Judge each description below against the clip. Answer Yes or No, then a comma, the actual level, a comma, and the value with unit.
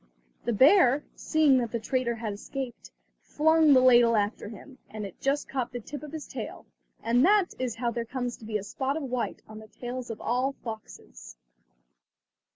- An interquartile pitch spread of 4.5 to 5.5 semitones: No, average, 3.2 semitones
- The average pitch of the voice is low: No, high, 245 Hz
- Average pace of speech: Yes, average, 190 wpm